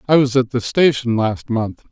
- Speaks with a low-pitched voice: Yes, low, 120 Hz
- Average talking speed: No, fast, 220 wpm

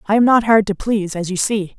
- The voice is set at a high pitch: Yes, high, 205 Hz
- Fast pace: Yes, fast, 305 wpm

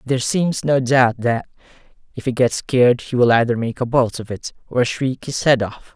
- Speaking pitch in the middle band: No, low, 125 Hz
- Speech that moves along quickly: Yes, fast, 220 wpm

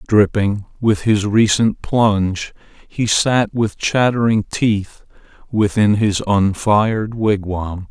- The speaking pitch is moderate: No, low, 105 Hz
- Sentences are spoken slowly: Yes, slow, 105 wpm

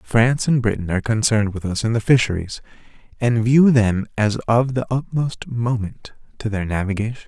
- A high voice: No, low, 115 Hz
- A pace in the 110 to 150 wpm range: No, average, 175 wpm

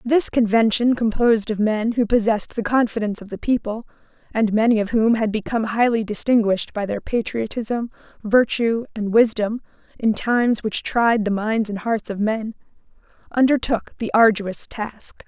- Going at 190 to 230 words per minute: No, average, 155 wpm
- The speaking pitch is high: Yes, high, 220 Hz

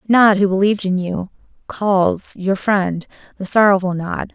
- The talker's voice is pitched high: Yes, high, 195 Hz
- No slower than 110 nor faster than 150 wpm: Yes, average, 140 wpm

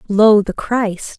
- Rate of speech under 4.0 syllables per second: Yes, 3.0 syllables/s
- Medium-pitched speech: No, high, 210 Hz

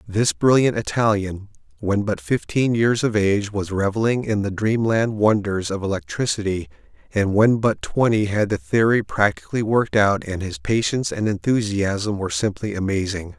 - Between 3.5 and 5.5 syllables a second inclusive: Yes, 5.0 syllables/s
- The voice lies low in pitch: Yes, low, 105 Hz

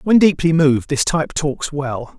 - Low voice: No, medium, 150 Hz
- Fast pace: No, average, 190 wpm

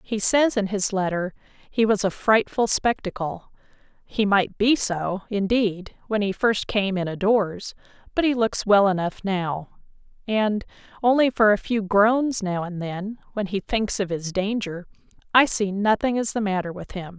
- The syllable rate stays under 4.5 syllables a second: Yes, 4.3 syllables/s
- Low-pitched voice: No, high, 205 Hz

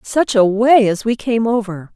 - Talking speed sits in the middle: No, fast, 215 wpm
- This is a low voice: No, high, 220 Hz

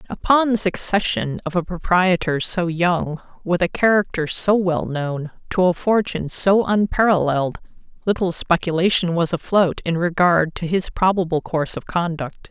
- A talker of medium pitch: Yes, medium, 175 Hz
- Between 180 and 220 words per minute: No, average, 150 wpm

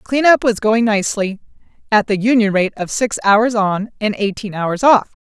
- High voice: Yes, high, 215 Hz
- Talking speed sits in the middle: Yes, average, 185 wpm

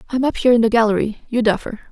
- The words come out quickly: Yes, fast, 250 wpm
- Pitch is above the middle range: Yes, high, 230 Hz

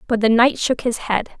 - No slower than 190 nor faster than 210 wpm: No, fast, 255 wpm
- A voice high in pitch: Yes, high, 235 Hz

